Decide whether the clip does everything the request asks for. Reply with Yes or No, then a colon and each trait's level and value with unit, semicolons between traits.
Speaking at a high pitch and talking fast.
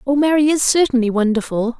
No: very high, 260 Hz; average, 170 wpm